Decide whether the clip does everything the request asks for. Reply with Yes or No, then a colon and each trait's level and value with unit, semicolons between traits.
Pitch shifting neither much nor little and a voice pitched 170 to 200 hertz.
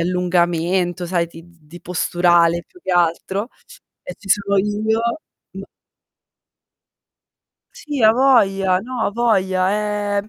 Yes: average, 3.1 semitones; high, 190 Hz